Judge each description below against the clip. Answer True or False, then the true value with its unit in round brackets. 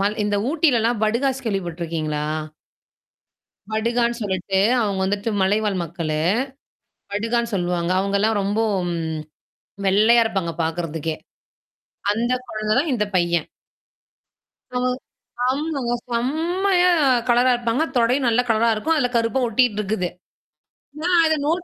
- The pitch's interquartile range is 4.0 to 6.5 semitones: True (4.3 semitones)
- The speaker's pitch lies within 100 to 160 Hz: False (225 Hz)